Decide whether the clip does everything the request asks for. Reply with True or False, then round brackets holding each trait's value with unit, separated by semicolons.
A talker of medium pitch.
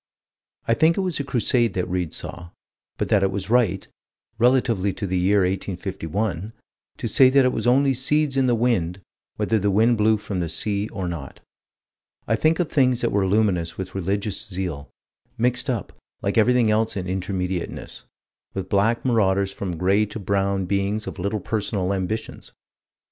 False (100 Hz)